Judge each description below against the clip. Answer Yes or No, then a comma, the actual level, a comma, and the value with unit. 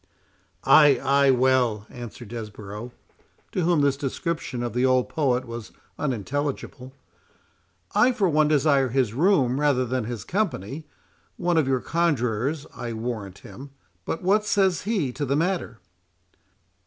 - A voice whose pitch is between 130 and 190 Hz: Yes, low, 135 Hz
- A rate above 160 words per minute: No, slow, 135 wpm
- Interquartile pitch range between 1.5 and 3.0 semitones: No, average, 4.3 semitones